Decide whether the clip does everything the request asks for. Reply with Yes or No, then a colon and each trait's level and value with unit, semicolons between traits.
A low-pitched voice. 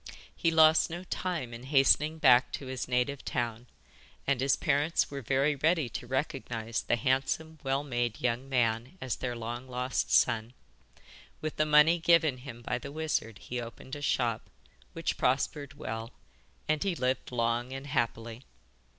Yes: low, 130 Hz